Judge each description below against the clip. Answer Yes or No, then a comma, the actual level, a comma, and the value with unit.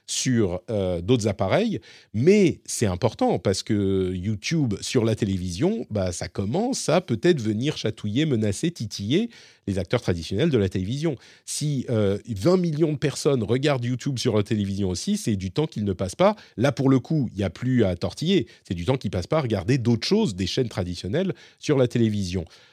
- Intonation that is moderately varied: No, wide, 6.7 semitones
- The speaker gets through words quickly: No, average, 195 wpm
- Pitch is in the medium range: No, low, 115 Hz